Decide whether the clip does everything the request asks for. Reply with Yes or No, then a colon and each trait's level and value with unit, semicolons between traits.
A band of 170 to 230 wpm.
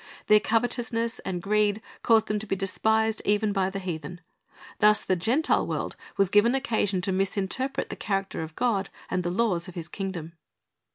Yes: average, 175 wpm